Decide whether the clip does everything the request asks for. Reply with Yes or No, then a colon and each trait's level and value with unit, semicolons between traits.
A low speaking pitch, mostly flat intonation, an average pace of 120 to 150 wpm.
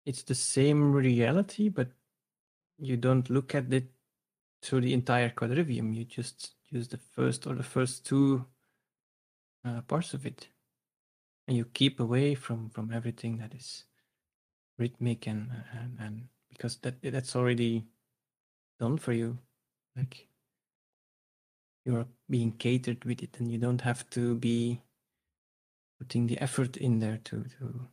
Yes: low, 120 Hz; narrow, 2.0 semitones; average, 140 wpm